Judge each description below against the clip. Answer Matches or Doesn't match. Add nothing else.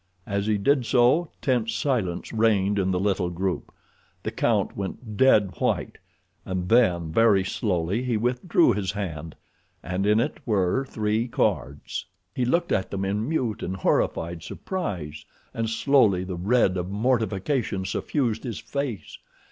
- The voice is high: Doesn't match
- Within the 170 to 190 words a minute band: Doesn't match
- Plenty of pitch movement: Doesn't match